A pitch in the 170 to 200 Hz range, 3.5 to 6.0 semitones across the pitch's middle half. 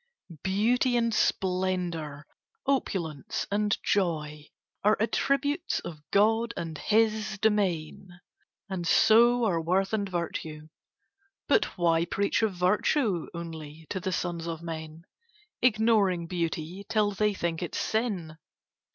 Yes: medium, 185 Hz; average, 4.5 semitones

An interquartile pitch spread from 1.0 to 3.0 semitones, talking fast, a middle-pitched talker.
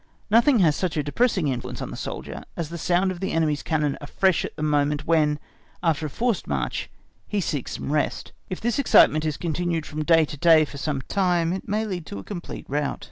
No: average, 3.7 semitones; fast, 220 wpm; medium, 160 Hz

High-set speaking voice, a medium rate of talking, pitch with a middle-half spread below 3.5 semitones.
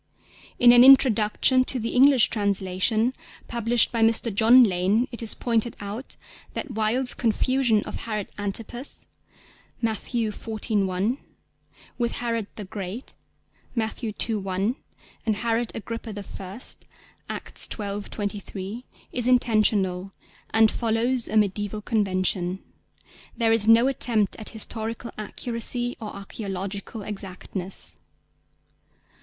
No: high, 220 Hz; slow, 115 wpm; average, 2.8 semitones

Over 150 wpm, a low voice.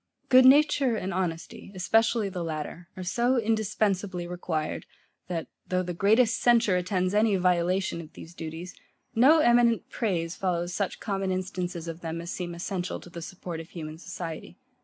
No: average, 160 wpm; medium, 185 Hz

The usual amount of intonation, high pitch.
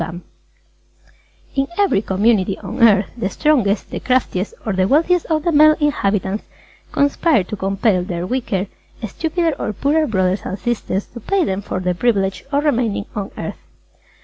No: wide, 6.9 semitones; high, 215 Hz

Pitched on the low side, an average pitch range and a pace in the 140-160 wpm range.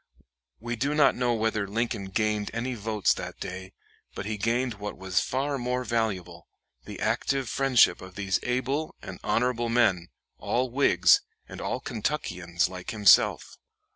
Yes: low, 115 Hz; average, 4.2 semitones; average, 150 wpm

